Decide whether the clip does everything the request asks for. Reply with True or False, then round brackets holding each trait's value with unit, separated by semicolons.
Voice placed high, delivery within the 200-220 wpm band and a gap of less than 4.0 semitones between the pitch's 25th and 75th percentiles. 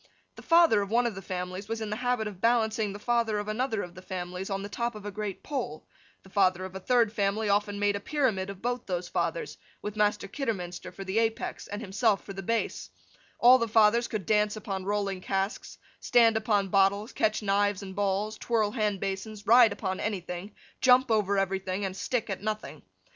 True (205 Hz; 205 wpm; 2.5 semitones)